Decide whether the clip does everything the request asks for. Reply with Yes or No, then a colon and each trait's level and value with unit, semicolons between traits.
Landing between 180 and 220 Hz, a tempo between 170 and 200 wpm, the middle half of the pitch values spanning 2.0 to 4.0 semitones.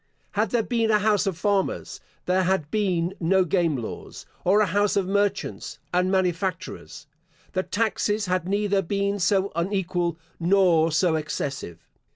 No: high, 190 Hz; average, 150 wpm; average, 2.9 semitones